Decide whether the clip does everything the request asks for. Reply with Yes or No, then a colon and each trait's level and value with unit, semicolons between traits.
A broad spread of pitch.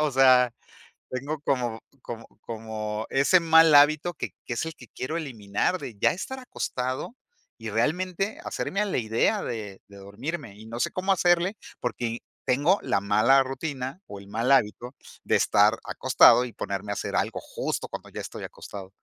Yes: wide, 6.4 semitones